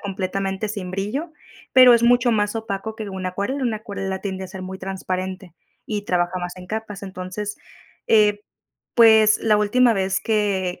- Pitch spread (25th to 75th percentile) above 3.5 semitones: No, narrow, 2.6 semitones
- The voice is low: No, high, 200 Hz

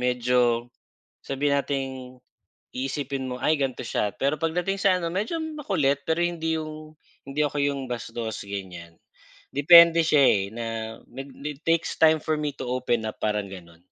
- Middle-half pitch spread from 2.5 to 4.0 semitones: No, average, 4.7 semitones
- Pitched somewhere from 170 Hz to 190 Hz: No, medium, 140 Hz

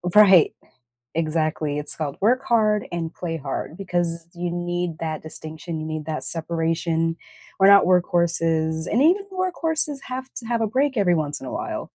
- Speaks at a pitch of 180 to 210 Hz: No, medium, 170 Hz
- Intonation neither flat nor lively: Yes, average, 4.8 semitones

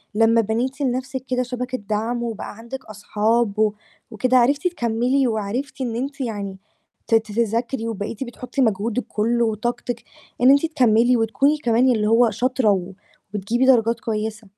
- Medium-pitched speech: No, high, 235 Hz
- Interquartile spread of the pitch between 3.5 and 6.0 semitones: No, average, 2.7 semitones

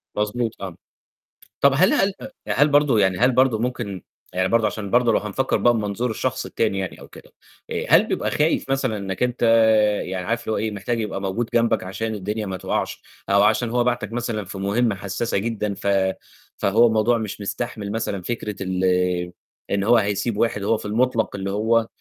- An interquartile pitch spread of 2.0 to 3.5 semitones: Yes, average, 3.1 semitones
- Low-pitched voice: Yes, low, 110 Hz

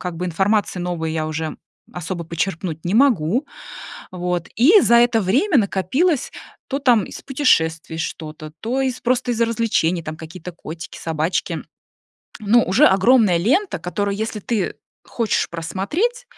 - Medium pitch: No, high, 195 Hz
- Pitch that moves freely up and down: Yes, wide, 6.4 semitones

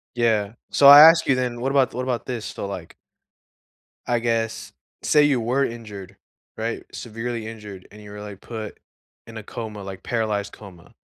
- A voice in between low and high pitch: No, low, 115 Hz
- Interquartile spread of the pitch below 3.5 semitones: Yes, average, 2.9 semitones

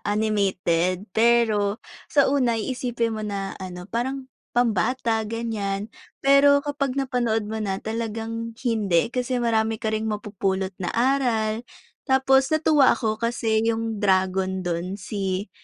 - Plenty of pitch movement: No, average, 3.4 semitones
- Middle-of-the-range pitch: No, high, 220 Hz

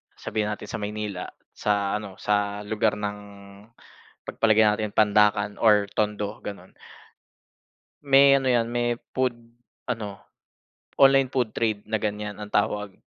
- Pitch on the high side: No, low, 105 Hz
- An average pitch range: No, narrow, 1.6 semitones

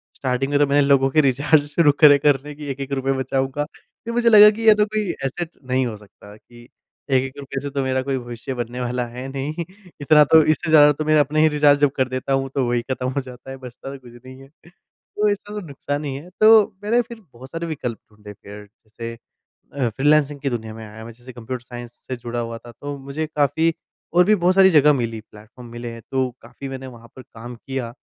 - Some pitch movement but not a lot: Yes, average, 3.5 semitones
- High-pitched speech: No, low, 135 Hz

